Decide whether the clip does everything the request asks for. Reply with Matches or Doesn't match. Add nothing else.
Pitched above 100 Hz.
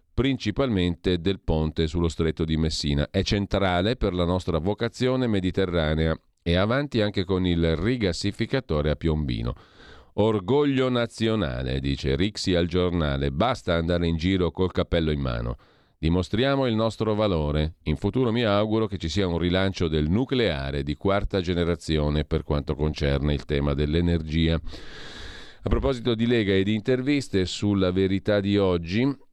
Doesn't match